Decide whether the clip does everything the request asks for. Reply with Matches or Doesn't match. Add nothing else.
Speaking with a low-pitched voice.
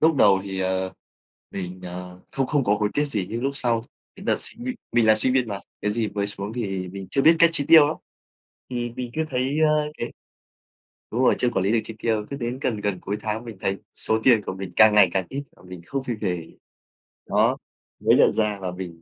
Matches